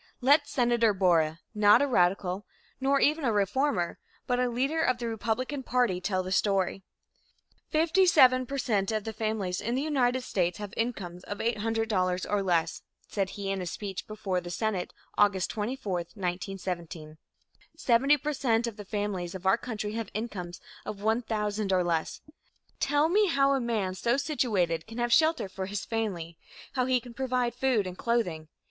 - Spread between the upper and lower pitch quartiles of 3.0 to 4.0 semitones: No, average, 5.0 semitones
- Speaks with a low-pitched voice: No, high, 215 Hz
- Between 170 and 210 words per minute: Yes, average, 175 wpm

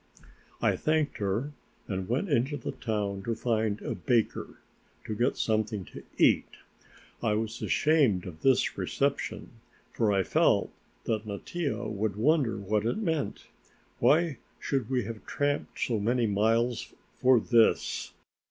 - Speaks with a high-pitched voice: No, low, 115 Hz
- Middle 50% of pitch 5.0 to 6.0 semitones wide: No, average, 4.4 semitones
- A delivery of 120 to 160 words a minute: Yes, average, 140 wpm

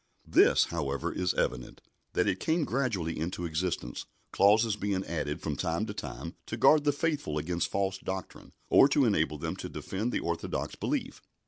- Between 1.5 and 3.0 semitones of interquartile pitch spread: No, wide, 5.4 semitones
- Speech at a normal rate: Yes, average, 175 wpm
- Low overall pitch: Yes, very low, 95 Hz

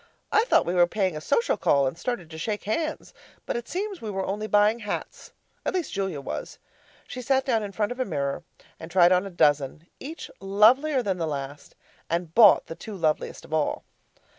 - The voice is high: Yes, high, 195 Hz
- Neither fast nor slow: No, fast, 210 wpm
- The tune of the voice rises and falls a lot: Yes, wide, 6.5 semitones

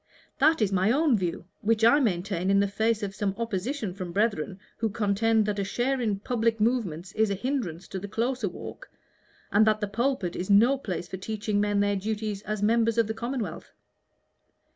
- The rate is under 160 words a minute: No, average, 195 wpm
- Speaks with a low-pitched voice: No, high, 210 Hz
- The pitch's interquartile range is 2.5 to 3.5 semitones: Yes, average, 2.8 semitones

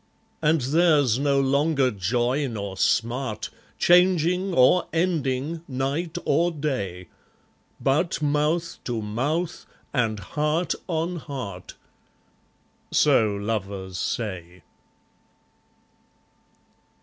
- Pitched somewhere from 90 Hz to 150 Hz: Yes, medium, 140 Hz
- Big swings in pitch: Yes, wide, 6.7 semitones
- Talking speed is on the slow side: Yes, slow, 85 wpm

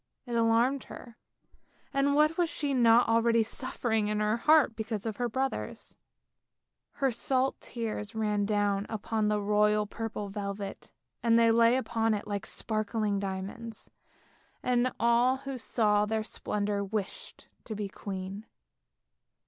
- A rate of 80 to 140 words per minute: Yes, slow, 135 wpm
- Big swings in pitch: No, narrow, 2.5 semitones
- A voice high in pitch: Yes, high, 225 Hz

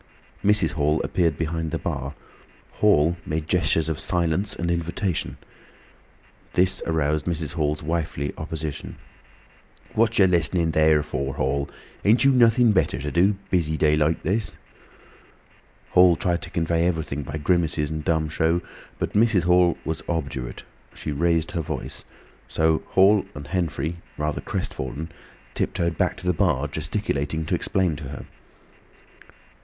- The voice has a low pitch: Yes, very low, 80 Hz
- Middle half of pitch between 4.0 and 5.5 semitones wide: No, average, 2.9 semitones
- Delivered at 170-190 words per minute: No, average, 145 wpm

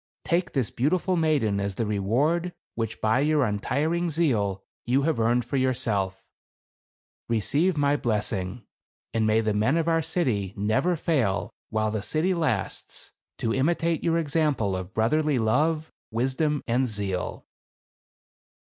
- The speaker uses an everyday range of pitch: No, wide, 6.5 semitones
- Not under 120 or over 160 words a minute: Yes, average, 140 wpm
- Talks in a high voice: No, low, 125 Hz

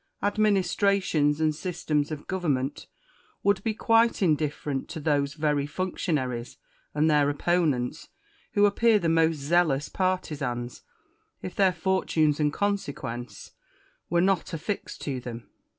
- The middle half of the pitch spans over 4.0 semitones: Yes, average, 4.7 semitones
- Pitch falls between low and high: Yes, medium, 155 Hz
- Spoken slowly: Yes, slow, 120 wpm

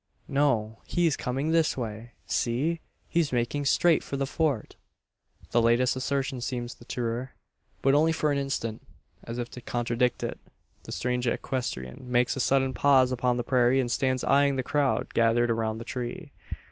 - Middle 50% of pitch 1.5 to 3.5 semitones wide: Yes, average, 2.7 semitones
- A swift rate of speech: No, average, 170 wpm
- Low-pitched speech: Yes, low, 125 Hz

